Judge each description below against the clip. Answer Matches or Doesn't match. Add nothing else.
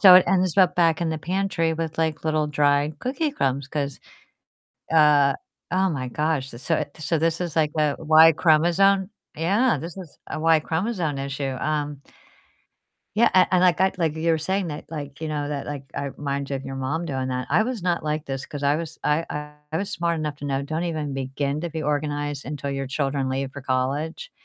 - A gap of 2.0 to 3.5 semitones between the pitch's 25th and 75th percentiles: Matches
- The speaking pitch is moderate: Matches